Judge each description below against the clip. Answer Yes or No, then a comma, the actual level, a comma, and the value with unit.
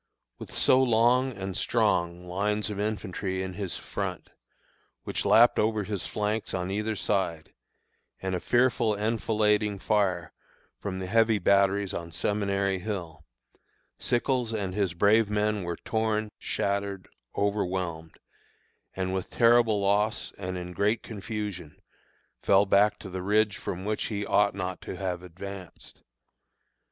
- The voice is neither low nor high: No, low, 100 Hz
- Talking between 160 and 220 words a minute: No, slow, 135 wpm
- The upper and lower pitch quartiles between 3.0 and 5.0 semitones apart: No, narrow, 2.4 semitones